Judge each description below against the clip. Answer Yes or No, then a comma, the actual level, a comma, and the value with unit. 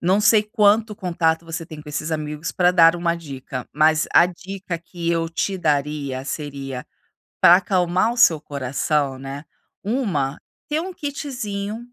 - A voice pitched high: No, medium, 170 Hz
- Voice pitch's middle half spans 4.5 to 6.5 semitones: Yes, average, 5.0 semitones